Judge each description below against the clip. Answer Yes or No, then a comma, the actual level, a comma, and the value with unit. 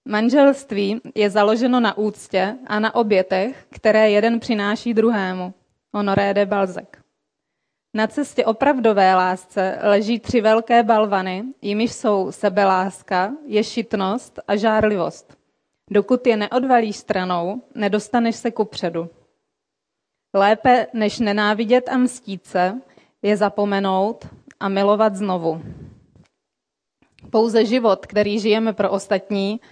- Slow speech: Yes, slow, 110 wpm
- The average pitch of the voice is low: No, high, 210 Hz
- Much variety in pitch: No, average, 2.7 semitones